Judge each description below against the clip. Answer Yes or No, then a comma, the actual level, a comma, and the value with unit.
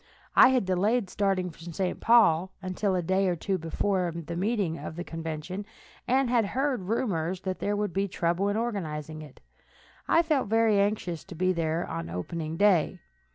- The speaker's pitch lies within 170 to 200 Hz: Yes, medium, 185 Hz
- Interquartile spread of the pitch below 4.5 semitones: Yes, average, 3.8 semitones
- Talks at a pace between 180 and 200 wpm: Yes, average, 185 wpm